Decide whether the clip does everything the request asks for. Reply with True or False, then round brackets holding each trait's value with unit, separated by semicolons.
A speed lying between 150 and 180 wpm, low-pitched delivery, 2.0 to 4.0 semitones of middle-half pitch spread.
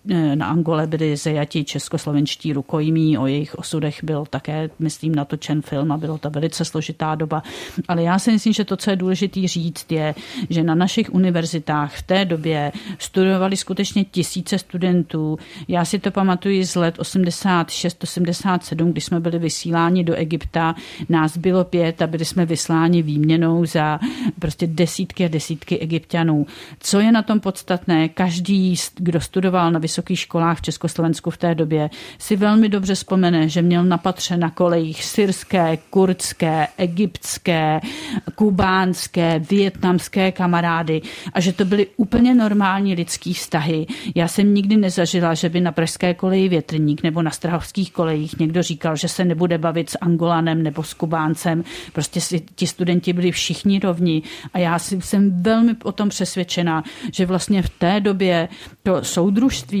False (155 wpm; 170 Hz; 2.7 semitones)